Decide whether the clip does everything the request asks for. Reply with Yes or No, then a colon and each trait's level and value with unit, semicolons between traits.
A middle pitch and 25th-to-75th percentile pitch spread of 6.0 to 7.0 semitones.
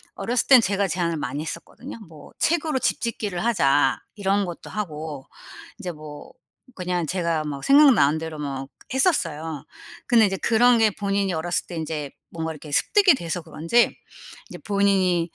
No: medium, 175 Hz; average, 5.3 semitones